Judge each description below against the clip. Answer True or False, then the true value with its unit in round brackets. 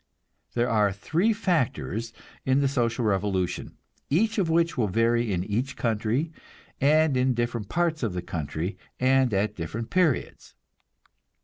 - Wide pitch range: True (6.4 semitones)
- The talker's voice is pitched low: True (120 Hz)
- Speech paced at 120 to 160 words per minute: True (140 wpm)